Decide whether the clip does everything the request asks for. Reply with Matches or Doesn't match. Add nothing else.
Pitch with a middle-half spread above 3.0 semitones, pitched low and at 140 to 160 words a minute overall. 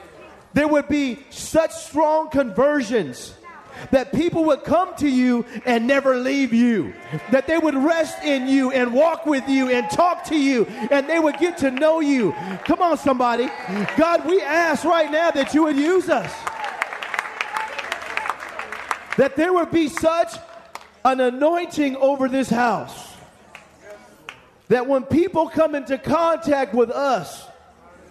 Doesn't match